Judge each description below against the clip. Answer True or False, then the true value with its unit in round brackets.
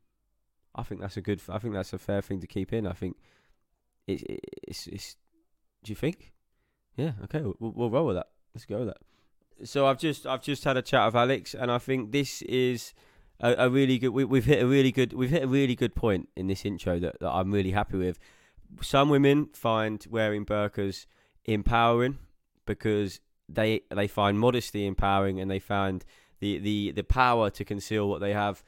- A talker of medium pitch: False (110 Hz)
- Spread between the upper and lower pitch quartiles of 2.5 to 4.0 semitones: False (4.4 semitones)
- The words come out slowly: False (205 wpm)